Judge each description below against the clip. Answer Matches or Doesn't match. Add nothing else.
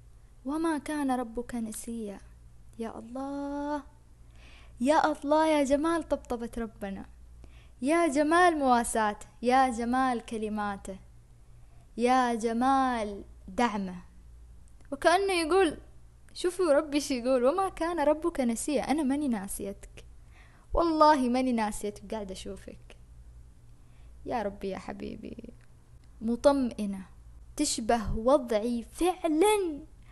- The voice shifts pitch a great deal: Matches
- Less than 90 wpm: Doesn't match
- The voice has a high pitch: Matches